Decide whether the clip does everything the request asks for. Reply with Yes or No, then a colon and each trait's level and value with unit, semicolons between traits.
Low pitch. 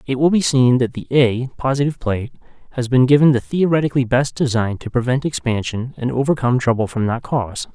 Yes: low, 130 Hz